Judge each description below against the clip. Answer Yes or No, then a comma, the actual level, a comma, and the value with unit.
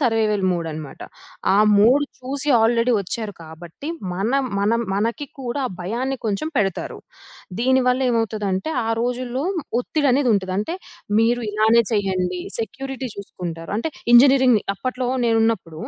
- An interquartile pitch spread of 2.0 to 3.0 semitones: No, average, 4.4 semitones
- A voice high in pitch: Yes, high, 225 Hz